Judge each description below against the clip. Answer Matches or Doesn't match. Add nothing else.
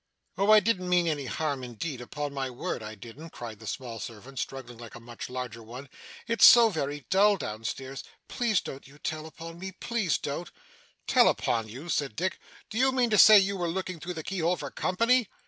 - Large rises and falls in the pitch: Matches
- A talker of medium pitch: Matches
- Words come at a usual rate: Doesn't match